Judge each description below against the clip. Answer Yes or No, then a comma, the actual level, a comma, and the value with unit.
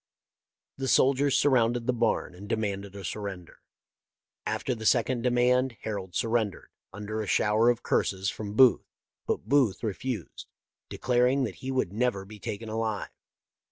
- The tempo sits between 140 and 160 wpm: Yes, average, 145 wpm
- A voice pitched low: Yes, low, 115 Hz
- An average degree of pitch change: Yes, average, 3.6 semitones